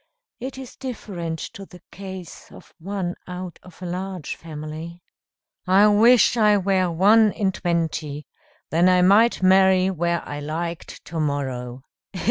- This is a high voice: No, medium, 180 Hz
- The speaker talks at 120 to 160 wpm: Yes, average, 140 wpm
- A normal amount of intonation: Yes, average, 3.2 semitones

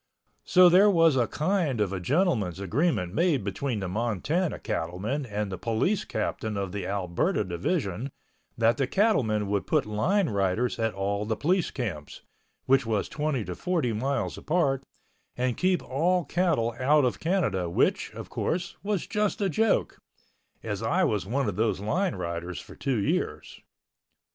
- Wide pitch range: Yes, wide, 8.7 semitones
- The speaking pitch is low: Yes, low, 125 Hz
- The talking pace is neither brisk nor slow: Yes, average, 165 wpm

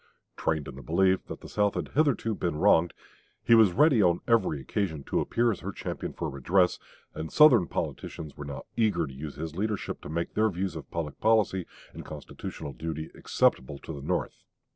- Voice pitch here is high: No, very low, 85 Hz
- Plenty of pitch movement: Yes, wide, 5.8 semitones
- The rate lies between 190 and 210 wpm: Yes, average, 195 wpm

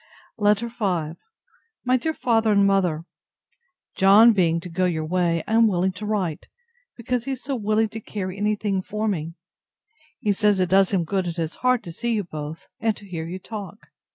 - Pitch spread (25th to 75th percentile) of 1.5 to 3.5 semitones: No, average, 3.9 semitones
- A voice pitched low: No, high, 200 Hz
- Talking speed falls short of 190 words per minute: No, average, 200 wpm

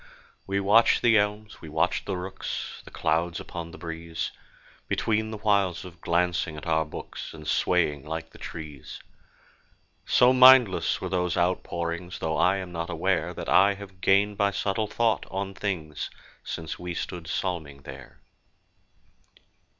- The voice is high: No, very low, 90 Hz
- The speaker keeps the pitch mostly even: No, average, 3.6 semitones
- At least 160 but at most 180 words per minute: No, average, 150 wpm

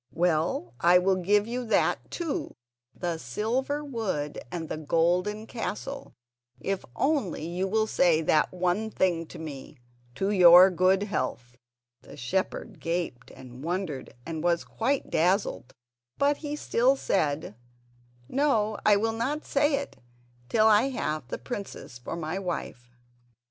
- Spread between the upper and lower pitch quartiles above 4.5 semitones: Yes, wide, 5.6 semitones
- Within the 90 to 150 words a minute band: Yes, average, 140 wpm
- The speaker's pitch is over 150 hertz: Yes, medium, 185 Hz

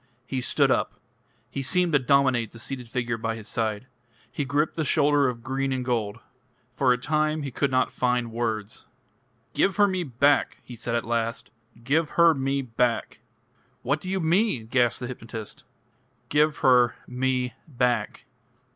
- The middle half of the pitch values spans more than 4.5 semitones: No, average, 3.5 semitones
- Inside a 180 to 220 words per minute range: No, average, 165 wpm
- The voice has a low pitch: Yes, low, 130 Hz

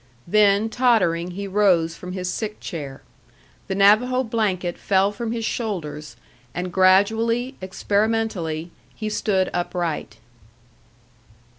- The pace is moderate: No, slow, 110 wpm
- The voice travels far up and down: No, average, 3.9 semitones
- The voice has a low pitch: No, high, 195 Hz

